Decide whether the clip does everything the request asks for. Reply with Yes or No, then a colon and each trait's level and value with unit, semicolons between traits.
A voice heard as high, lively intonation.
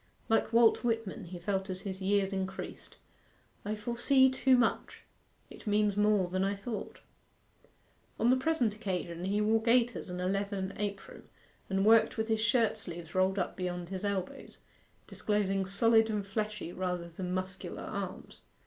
No: high, 200 Hz; average, 2.9 semitones